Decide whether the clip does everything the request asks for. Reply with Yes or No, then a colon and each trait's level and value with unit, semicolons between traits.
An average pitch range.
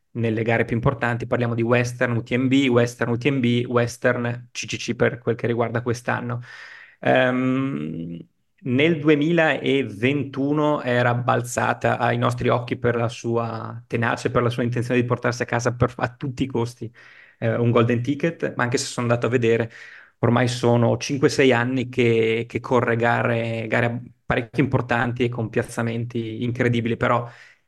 No: narrow, 1.4 semitones